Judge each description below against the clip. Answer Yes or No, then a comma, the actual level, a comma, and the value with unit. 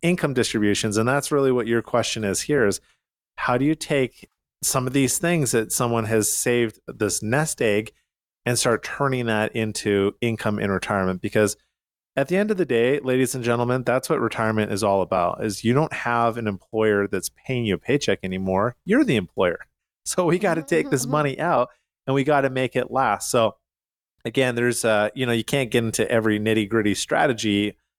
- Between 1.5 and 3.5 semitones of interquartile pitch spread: No, average, 4.1 semitones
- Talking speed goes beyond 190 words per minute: Yes, average, 200 wpm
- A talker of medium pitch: No, low, 120 Hz